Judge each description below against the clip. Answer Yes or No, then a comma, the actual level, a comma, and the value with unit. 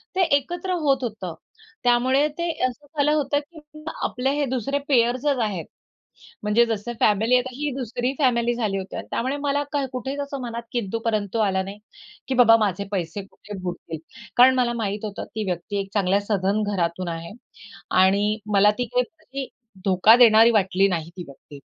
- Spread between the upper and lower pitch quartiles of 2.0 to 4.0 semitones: No, average, 4.9 semitones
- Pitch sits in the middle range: No, high, 230 Hz